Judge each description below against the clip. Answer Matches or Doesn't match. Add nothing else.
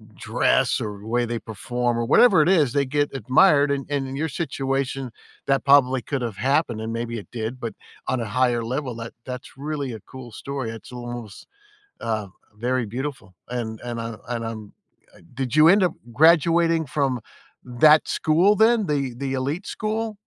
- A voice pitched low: Matches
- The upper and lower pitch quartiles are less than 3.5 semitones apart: Doesn't match